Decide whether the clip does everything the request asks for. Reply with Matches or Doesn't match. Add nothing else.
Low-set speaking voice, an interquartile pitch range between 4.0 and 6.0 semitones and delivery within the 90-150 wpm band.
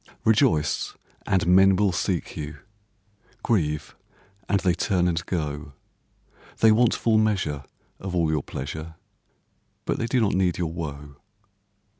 Matches